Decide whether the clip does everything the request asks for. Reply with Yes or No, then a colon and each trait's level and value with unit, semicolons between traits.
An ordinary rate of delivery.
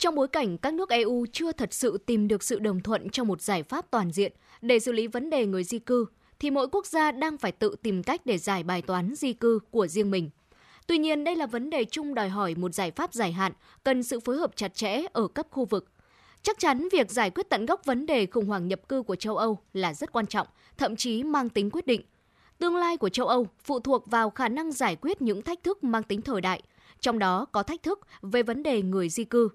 No: fast, 255 wpm